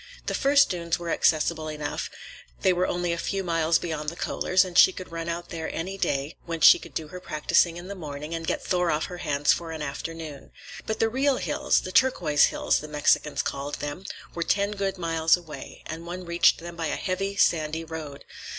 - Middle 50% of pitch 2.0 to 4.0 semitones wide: Yes, average, 2.8 semitones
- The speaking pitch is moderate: Yes, medium, 170 Hz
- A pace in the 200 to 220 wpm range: Yes, fast, 205 wpm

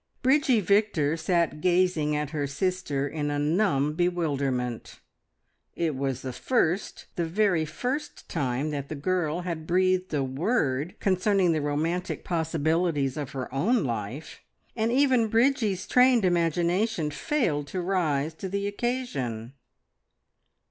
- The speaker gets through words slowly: Yes, slow, 130 wpm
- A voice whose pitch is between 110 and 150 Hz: No, medium, 170 Hz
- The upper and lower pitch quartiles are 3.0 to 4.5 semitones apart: No, average, 5.1 semitones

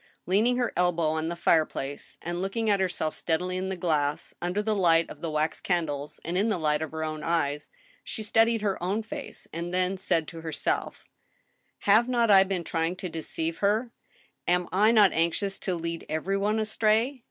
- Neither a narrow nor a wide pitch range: Yes, average, 4.2 semitones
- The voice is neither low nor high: Yes, medium, 180 Hz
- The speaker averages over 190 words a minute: Yes, average, 200 wpm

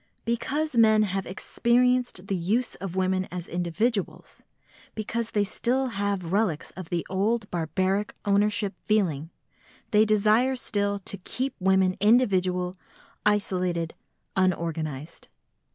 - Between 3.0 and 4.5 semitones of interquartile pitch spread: Yes, average, 3.3 semitones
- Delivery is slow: Yes, slow, 115 wpm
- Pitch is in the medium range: No, high, 200 Hz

